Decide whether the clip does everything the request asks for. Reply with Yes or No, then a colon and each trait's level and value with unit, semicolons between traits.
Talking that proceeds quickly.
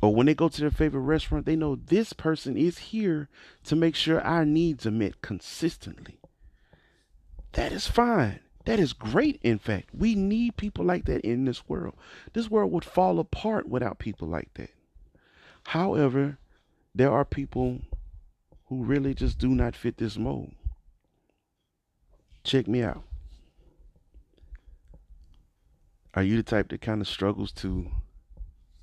No: average, 150 wpm